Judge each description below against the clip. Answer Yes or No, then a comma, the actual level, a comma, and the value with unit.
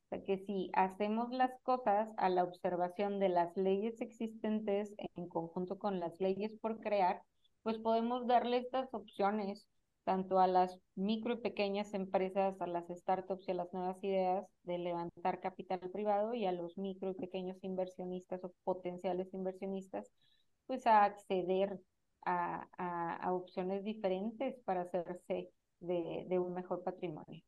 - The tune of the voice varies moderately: No, narrow, 2.2 semitones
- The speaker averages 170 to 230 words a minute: No, average, 155 wpm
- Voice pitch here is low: No, high, 190 Hz